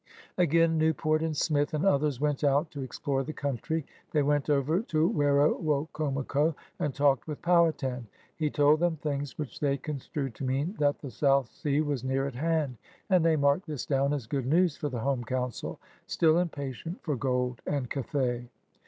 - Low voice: No, medium, 145 Hz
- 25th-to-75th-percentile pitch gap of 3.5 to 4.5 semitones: No, narrow, 2.5 semitones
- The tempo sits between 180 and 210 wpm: Yes, average, 185 wpm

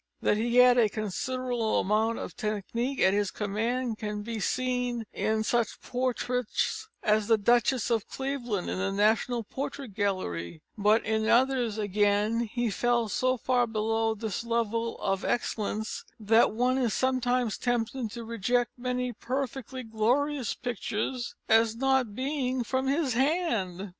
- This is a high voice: Yes, high, 235 Hz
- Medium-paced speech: Yes, average, 145 wpm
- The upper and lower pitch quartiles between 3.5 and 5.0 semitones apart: No, average, 2.8 semitones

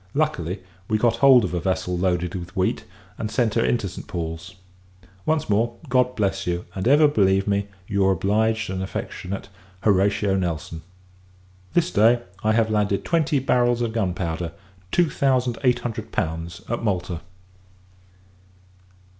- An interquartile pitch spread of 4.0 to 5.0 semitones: Yes, average, 4.4 semitones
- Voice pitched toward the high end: No, low, 100 Hz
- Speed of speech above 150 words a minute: No, average, 145 wpm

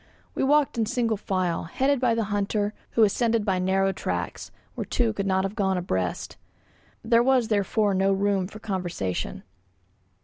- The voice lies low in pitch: No, high, 205 Hz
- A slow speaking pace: No, average, 165 wpm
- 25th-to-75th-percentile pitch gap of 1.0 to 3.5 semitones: Yes, average, 3.2 semitones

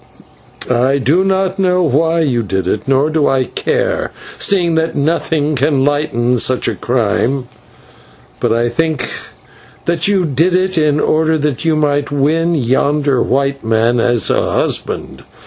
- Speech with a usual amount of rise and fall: Yes, average, 4.3 semitones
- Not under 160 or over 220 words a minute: No, average, 150 wpm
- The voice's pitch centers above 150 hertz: No, medium, 145 Hz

